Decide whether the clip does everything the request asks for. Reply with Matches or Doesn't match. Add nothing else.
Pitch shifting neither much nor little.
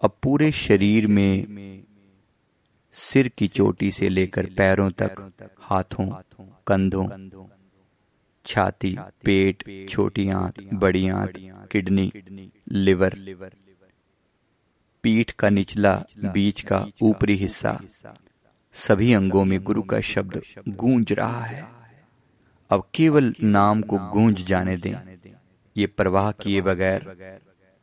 Doesn't match